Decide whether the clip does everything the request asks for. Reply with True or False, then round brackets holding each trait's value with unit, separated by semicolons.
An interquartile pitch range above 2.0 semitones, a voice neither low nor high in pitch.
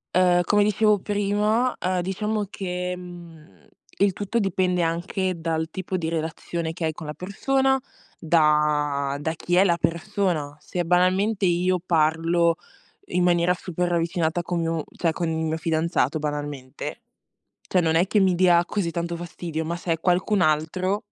True (2.4 semitones; 175 Hz)